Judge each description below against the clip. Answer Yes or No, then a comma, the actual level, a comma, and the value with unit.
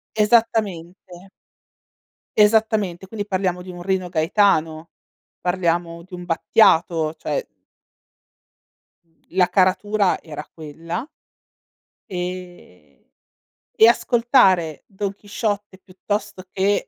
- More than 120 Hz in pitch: Yes, medium, 185 Hz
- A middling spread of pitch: Yes, average, 3.4 semitones